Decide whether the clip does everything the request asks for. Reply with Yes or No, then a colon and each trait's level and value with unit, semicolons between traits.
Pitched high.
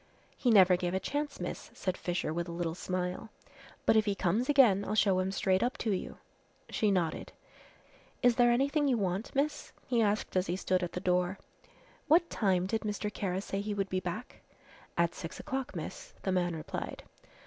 Yes: high, 195 Hz